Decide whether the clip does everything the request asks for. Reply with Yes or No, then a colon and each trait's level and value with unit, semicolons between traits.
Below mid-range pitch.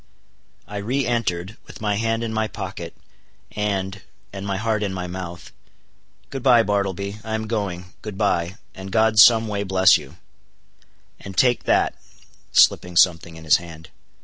Yes: low, 100 Hz